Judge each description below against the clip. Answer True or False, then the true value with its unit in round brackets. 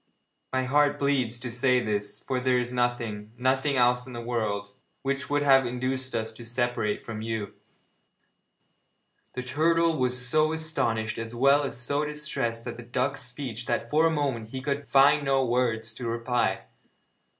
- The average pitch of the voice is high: False (125 Hz)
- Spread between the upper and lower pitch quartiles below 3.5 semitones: True (2.9 semitones)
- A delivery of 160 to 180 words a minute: True (170 wpm)